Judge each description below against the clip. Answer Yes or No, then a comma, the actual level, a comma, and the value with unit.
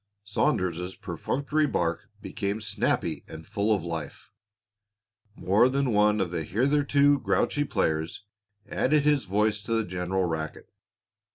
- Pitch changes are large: Yes, wide, 6.6 semitones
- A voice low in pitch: Yes, low, 105 Hz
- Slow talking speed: Yes, slow, 125 wpm